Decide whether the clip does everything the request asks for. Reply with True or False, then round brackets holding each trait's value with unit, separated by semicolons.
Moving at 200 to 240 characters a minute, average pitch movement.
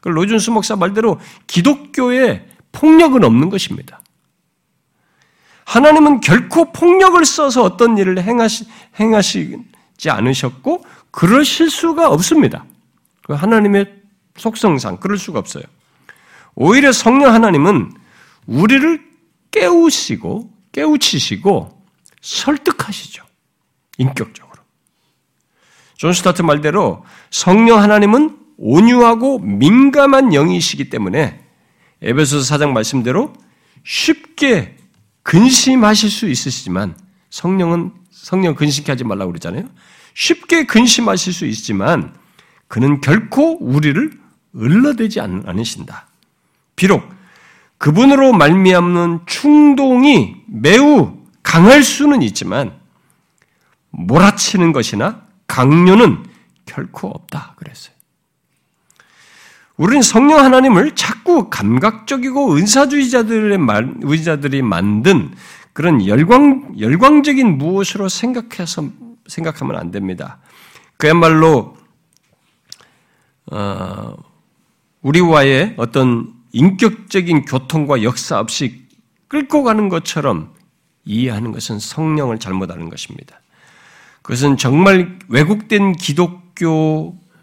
False (235 characters per minute; 8.9 semitones)